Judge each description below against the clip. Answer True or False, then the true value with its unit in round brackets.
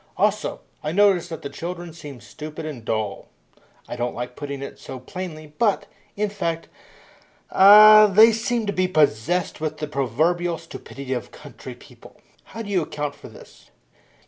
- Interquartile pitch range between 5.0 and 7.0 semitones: True (5.4 semitones)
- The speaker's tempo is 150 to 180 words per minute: True (165 wpm)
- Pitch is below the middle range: False (160 Hz)